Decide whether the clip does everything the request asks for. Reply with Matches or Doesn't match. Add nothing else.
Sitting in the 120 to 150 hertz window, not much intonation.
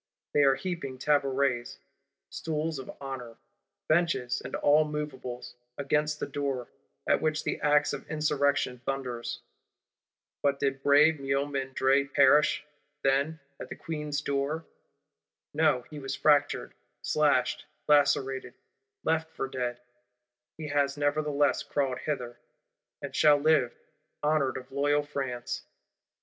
Matches